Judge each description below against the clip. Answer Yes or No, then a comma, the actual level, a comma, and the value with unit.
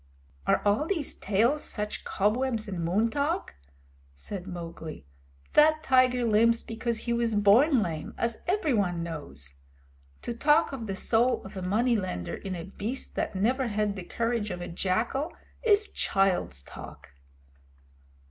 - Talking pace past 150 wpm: No, average, 145 wpm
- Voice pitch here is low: No, high, 220 Hz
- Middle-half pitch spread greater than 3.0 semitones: Yes, average, 5.2 semitones